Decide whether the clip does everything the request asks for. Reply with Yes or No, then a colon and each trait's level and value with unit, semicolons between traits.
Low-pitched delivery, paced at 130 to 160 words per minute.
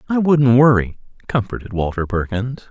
Yes: low, 120 Hz; slow, 135 wpm